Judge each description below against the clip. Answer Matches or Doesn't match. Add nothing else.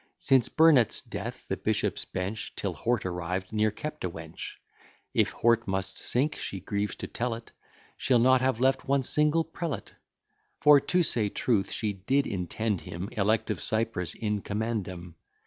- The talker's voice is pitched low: Matches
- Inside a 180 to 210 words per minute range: Doesn't match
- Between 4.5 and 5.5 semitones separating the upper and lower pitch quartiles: Matches